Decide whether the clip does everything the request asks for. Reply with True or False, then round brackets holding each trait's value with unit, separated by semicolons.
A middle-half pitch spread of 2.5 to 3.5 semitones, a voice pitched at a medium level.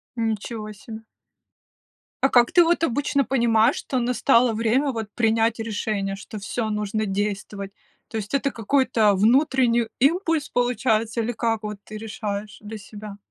False (2.8 semitones; 225 Hz)